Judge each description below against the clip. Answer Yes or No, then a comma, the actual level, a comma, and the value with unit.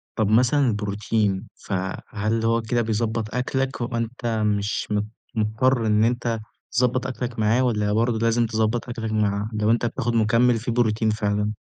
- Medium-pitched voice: No, low, 115 Hz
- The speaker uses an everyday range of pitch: No, narrow, 2.0 semitones